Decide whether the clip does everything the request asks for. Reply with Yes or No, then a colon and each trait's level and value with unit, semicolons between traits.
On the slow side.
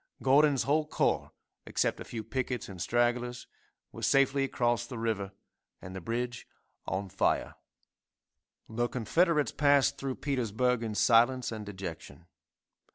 Yes: slow, 130 wpm